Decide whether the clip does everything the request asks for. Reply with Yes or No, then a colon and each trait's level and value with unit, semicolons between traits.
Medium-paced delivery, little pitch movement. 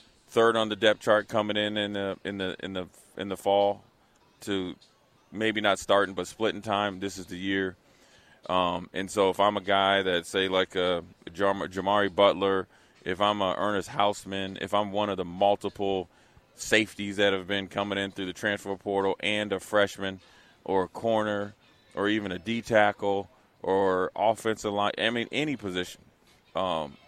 Yes: average, 175 wpm; narrow, 1.5 semitones